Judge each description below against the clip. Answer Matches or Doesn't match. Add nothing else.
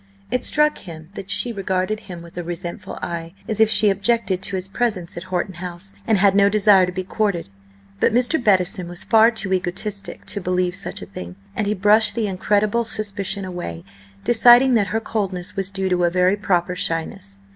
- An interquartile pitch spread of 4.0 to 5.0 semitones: Doesn't match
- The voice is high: Matches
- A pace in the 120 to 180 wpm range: Doesn't match